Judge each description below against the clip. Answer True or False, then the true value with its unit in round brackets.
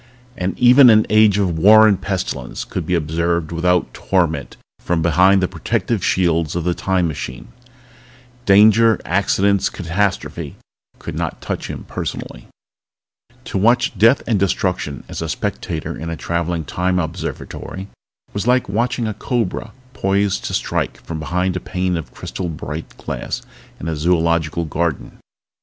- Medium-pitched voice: False (90 Hz)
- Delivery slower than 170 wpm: True (150 wpm)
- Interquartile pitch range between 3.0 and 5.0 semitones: True (3.4 semitones)